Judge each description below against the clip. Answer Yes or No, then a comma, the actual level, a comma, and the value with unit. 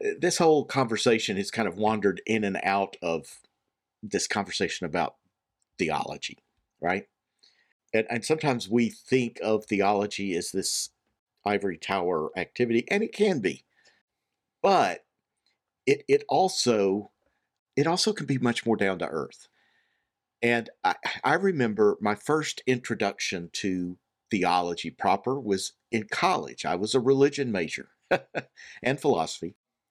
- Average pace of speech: No, slow, 130 wpm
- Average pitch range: No, wide, 5.7 semitones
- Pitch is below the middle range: Yes, low, 115 Hz